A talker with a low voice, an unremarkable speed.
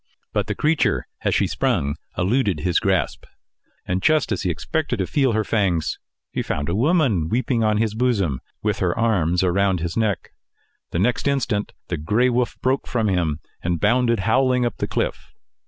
Yes: low, 105 Hz; average, 180 wpm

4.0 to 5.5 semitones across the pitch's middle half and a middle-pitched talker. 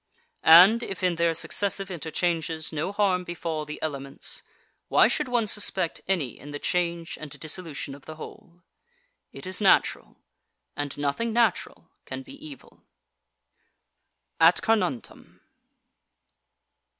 Yes: average, 4.4 semitones; medium, 175 Hz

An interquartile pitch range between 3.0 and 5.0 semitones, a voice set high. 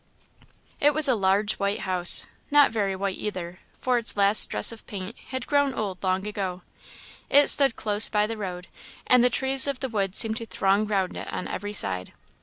Yes: average, 4.6 semitones; high, 210 Hz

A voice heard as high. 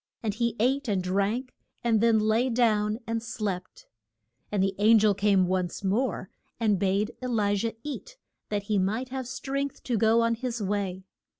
Yes: high, 215 Hz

